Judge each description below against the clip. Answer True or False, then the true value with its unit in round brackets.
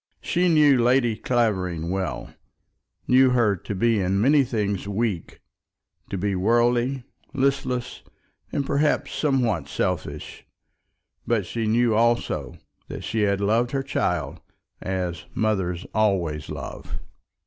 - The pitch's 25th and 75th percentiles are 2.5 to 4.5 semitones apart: False (4.9 semitones)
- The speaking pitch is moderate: False (110 Hz)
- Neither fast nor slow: False (120 wpm)